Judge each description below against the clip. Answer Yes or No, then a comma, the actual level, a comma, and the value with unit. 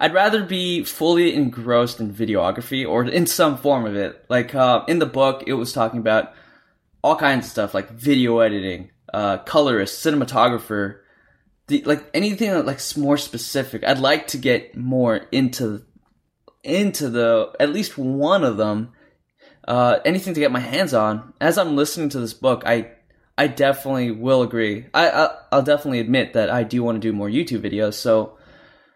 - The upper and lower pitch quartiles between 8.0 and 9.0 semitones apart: No, average, 4.2 semitones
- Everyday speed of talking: Yes, average, 175 wpm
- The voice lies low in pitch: Yes, low, 125 Hz